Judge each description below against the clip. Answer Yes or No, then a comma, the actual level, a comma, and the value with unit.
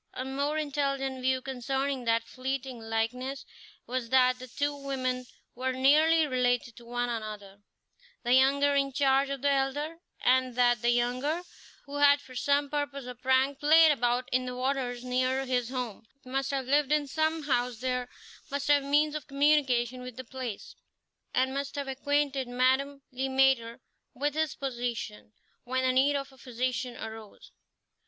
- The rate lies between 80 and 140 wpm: No, average, 165 wpm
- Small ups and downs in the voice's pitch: Yes, narrow, 2.1 semitones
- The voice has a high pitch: Yes, very high, 260 Hz